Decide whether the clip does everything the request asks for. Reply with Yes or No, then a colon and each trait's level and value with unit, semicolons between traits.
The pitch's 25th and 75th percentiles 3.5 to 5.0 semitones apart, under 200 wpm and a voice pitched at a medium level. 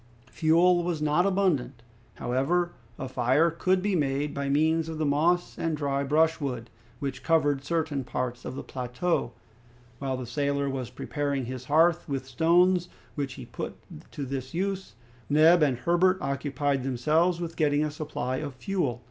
Yes: average, 3.9 semitones; average, 160 wpm; medium, 145 Hz